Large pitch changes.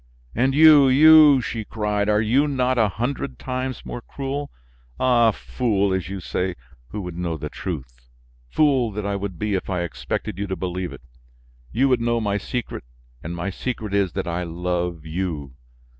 Yes: wide, 6.1 semitones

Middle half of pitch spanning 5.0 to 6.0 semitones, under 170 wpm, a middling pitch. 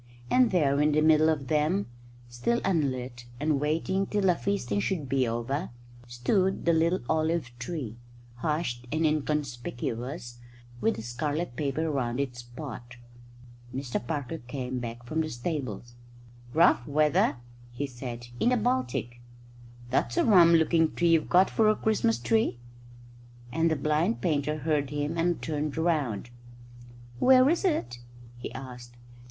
Yes: average, 5.3 semitones; average, 145 wpm; medium, 150 Hz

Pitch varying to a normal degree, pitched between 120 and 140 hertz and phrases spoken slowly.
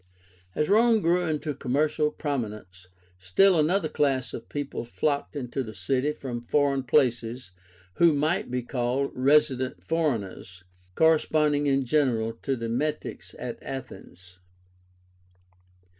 Yes: average, 4.1 semitones; low, 135 Hz; slow, 120 wpm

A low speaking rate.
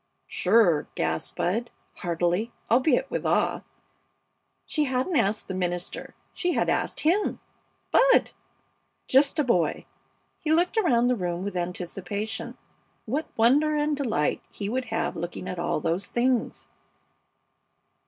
Yes: slow, 130 wpm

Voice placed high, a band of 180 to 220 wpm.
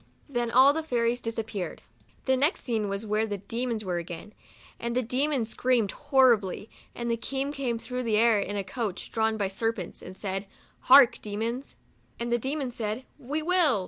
Yes: high, 235 Hz; average, 200 wpm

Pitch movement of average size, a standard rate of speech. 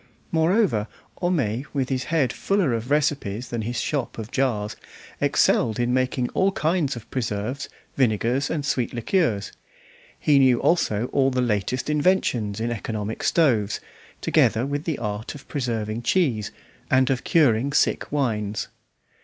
Yes: average, 4.6 semitones; average, 145 wpm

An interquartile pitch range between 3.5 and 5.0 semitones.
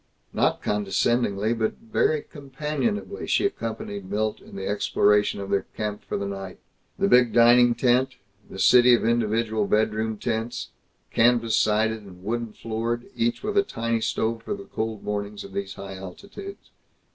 No: average, 2.8 semitones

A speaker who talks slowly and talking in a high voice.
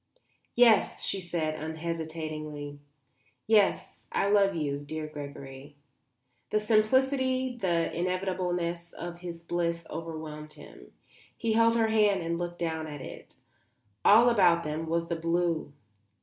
No: slow, 125 wpm; medium, 170 Hz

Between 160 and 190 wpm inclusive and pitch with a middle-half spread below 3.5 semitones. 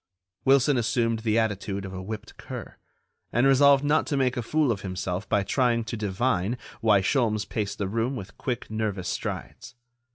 No: average, 175 wpm; average, 4.1 semitones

